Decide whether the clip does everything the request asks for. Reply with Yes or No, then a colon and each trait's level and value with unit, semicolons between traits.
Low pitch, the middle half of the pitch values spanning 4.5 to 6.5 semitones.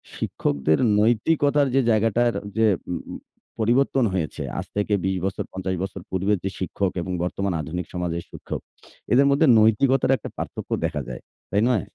Yes: low, 105 Hz; average, 4.9 semitones